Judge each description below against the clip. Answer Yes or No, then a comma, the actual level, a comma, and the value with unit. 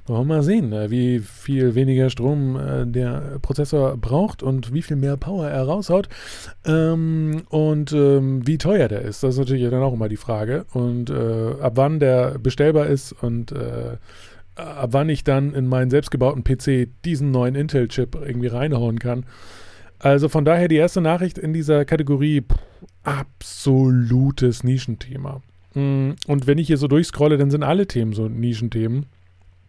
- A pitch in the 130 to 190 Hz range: Yes, low, 135 Hz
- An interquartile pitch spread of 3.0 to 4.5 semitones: Yes, average, 3.4 semitones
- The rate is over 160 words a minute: No, average, 150 wpm